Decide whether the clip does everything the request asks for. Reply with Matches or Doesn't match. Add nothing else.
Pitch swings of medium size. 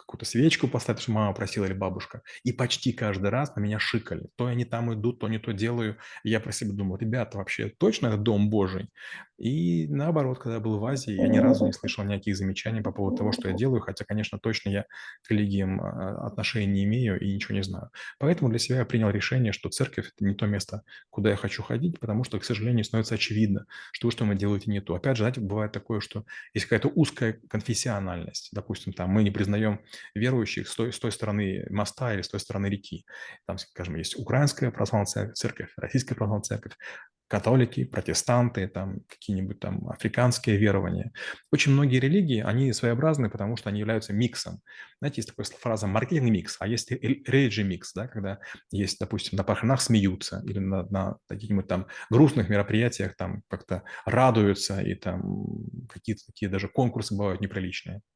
Matches